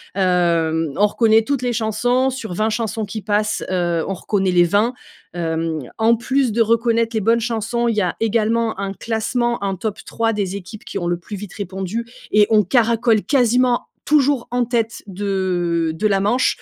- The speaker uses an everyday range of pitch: Yes, average, 3.5 semitones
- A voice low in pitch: No, high, 215 Hz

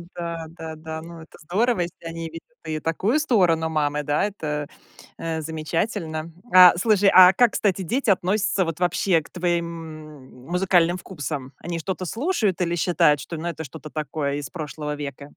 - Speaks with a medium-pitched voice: Yes, medium, 165 Hz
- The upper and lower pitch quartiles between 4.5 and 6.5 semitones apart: No, average, 2.9 semitones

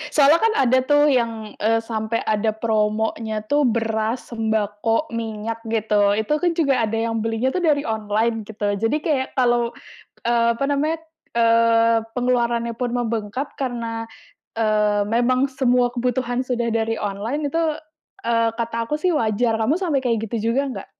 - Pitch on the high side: Yes, high, 230 Hz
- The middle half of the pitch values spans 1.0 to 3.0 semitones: Yes, narrow, 2.6 semitones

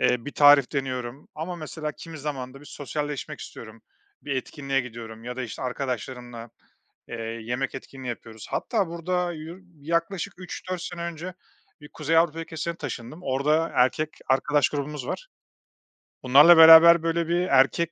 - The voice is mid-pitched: Yes, medium, 150 Hz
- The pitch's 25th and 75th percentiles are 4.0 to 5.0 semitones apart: Yes, average, 4.4 semitones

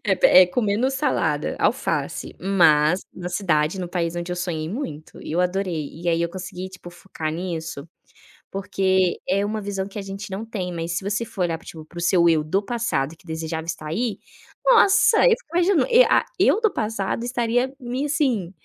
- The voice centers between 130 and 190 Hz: Yes, medium, 185 Hz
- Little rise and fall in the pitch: No, average, 4.7 semitones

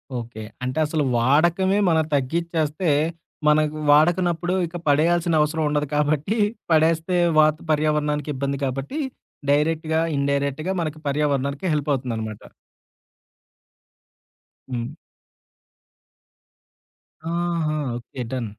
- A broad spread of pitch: No, average, 2.7 semitones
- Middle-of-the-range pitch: Yes, medium, 150 Hz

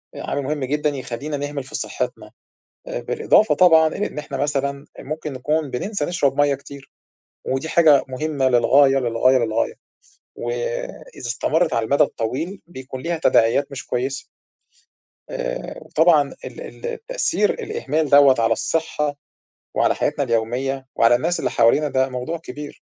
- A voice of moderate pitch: Yes, medium, 145 Hz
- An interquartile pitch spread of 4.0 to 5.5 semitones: No, average, 3.5 semitones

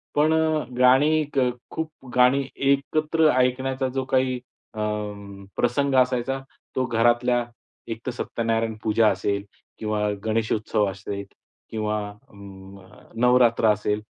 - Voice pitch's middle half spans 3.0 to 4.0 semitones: Yes, average, 3.3 semitones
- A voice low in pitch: Yes, low, 125 Hz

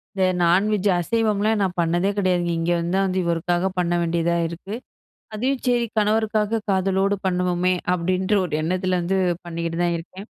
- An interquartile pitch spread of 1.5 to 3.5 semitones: Yes, average, 2.8 semitones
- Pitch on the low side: No, medium, 185 Hz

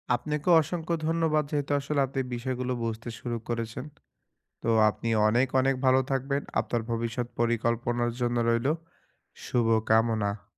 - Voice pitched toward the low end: Yes, low, 120 Hz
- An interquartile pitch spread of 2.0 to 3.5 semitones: Yes, average, 3.0 semitones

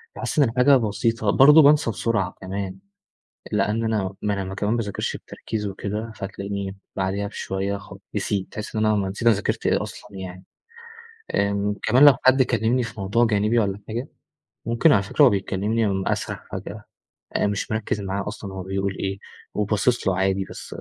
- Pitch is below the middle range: Yes, low, 105 Hz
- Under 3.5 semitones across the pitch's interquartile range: Yes, average, 2.8 semitones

